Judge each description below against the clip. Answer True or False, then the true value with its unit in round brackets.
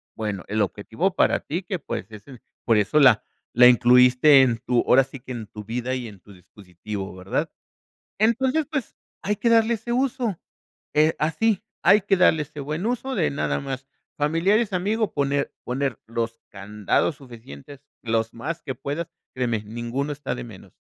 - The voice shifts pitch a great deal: True (7.8 semitones)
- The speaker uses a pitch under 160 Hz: True (135 Hz)